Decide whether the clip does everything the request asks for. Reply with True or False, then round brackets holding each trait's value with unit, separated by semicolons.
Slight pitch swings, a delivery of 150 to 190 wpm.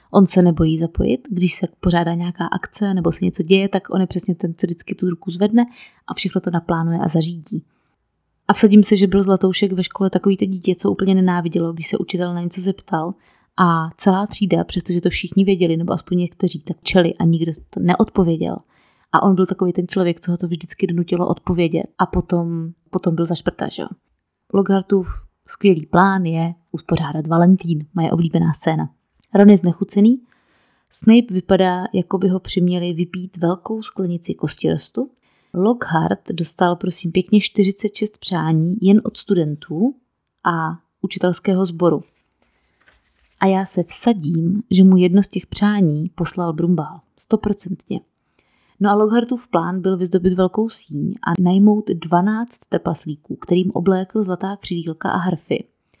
True (2.3 semitones; 160 wpm)